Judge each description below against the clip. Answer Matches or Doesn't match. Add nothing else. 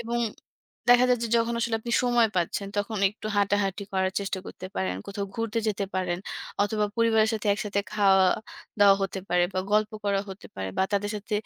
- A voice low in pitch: Doesn't match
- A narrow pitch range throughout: Matches